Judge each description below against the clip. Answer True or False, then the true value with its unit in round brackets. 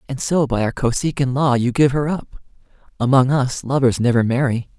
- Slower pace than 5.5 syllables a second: True (5.3 syllables/s)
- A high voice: False (130 Hz)